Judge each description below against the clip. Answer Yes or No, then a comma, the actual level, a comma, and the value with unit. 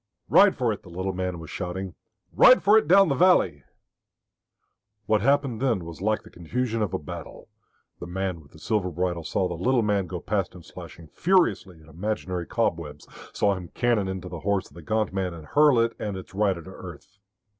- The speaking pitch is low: Yes, very low, 95 Hz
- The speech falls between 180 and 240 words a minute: Yes, fast, 205 wpm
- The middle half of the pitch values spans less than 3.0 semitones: No, average, 4.2 semitones